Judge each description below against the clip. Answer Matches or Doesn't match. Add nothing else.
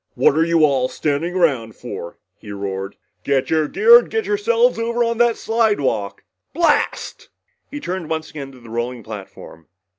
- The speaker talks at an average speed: Matches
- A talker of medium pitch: Matches